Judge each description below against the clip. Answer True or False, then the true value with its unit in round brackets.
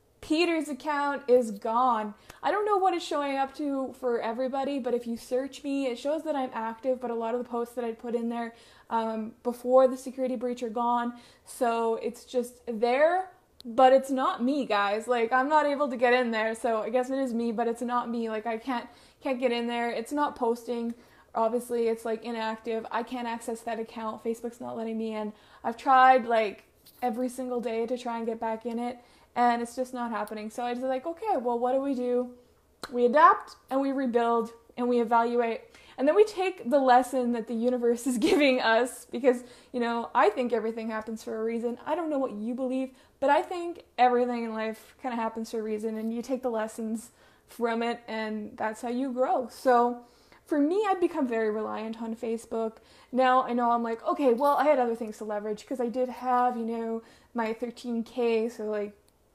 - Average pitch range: False (2.1 semitones)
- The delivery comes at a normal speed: False (215 wpm)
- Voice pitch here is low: False (240 Hz)